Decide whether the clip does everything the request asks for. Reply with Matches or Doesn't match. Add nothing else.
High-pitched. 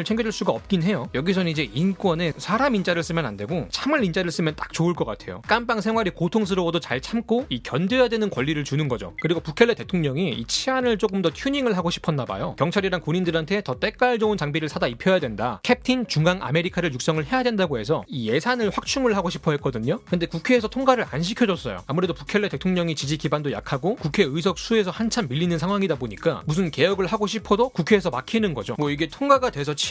Doesn't match